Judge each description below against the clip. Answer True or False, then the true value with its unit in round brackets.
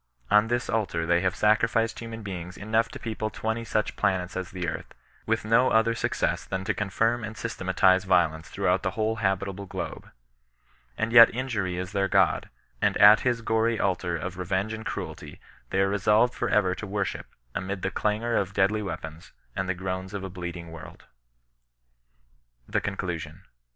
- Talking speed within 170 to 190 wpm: True (175 wpm)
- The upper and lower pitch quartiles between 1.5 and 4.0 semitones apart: True (3.2 semitones)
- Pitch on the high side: False (100 Hz)